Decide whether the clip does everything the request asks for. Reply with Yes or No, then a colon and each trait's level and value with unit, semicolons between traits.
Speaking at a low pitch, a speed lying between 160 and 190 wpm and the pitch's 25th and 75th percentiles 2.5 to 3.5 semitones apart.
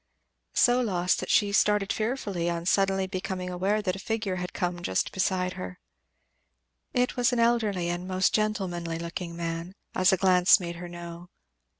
No: medium, 185 Hz; average, 170 wpm; average, 2.8 semitones